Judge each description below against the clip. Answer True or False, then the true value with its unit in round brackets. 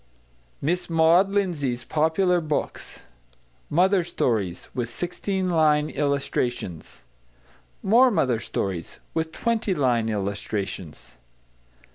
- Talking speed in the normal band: False (90 wpm)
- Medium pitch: True (150 Hz)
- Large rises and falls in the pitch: True (7.4 semitones)